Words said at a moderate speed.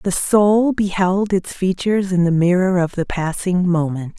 Yes: average, 170 wpm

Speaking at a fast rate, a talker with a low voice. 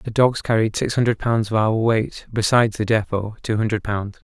Yes: fast, 210 wpm; low, 110 Hz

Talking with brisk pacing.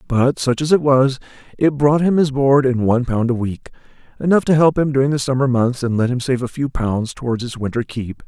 Yes: fast, 240 wpm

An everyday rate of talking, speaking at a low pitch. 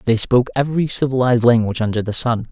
Yes: average, 190 wpm; low, 120 Hz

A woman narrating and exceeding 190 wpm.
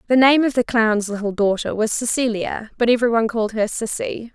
Yes: female; fast, 205 wpm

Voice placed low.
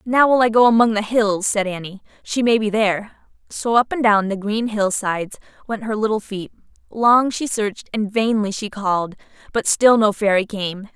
No: high, 215 Hz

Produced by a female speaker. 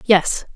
Yes: female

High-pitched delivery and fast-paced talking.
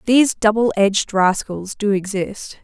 No: high, 205 Hz; slow, 135 wpm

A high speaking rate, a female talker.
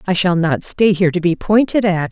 Yes: fast, 255 wpm; female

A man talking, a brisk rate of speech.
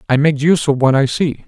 Yes: male; fast, 285 wpm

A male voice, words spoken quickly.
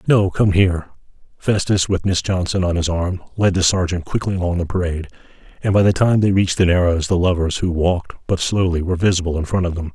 Yes: male; fast, 215 wpm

